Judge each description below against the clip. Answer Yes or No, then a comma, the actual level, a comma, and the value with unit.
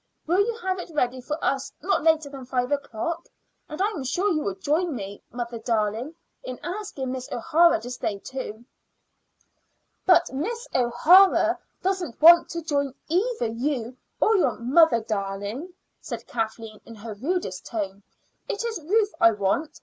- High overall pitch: Yes, very high, 275 Hz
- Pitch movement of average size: No, wide, 7.0 semitones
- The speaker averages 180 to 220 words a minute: No, average, 160 wpm